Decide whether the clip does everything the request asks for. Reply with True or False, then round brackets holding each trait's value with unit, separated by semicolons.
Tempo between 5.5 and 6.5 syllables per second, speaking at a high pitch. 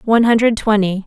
True (6.2 syllables/s; 215 Hz)